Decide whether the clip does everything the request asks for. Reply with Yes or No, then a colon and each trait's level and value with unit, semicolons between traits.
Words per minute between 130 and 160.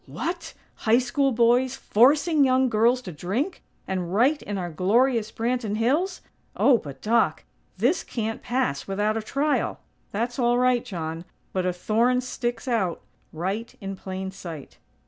Yes: average, 150 wpm